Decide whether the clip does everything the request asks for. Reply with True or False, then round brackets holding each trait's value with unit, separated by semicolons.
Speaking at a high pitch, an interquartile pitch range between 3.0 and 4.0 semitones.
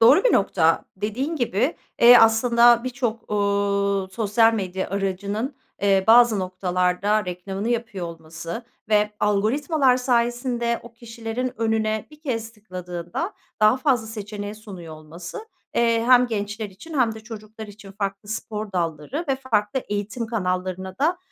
True (215 Hz; 3.4 semitones)